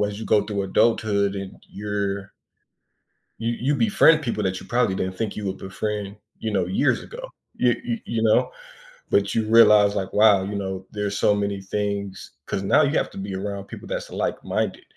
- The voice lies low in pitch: Yes, low, 105 Hz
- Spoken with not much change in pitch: Yes, narrow, 2.3 semitones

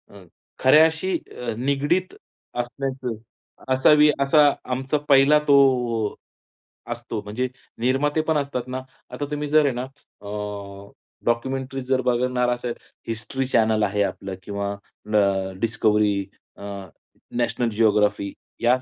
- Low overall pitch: Yes, low, 120 Hz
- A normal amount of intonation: Yes, average, 4.4 semitones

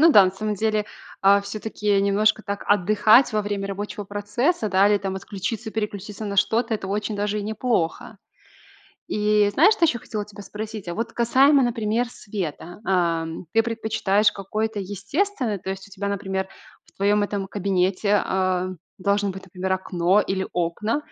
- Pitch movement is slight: Yes, narrow, 2.0 semitones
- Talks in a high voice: Yes, high, 205 Hz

